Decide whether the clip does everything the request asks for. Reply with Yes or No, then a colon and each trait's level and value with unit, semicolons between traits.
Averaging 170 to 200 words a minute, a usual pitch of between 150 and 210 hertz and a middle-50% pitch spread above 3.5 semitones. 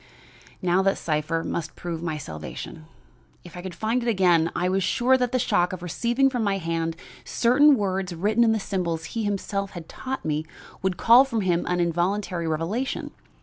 Yes: average, 190 wpm; medium, 185 Hz; average, 5.1 semitones